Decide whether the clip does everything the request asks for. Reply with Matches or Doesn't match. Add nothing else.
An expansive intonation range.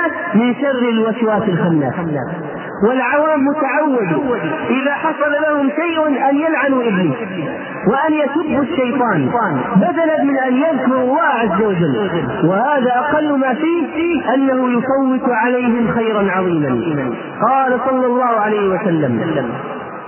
Matches